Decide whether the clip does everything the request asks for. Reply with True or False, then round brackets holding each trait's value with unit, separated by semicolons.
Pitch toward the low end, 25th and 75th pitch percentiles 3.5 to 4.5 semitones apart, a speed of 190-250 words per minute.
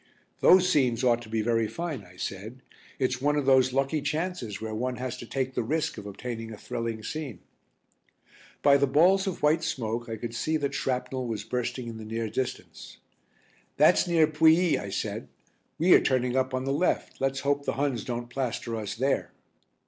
True (130 Hz; 4.0 semitones; 195 wpm)